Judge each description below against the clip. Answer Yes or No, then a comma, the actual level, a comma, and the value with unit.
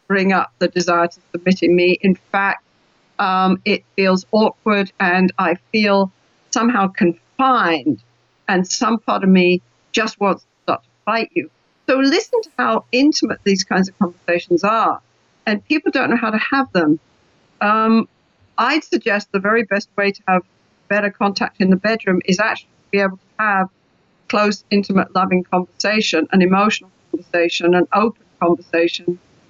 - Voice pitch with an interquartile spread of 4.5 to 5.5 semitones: No, average, 3.3 semitones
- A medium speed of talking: Yes, average, 165 wpm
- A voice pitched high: Yes, high, 195 Hz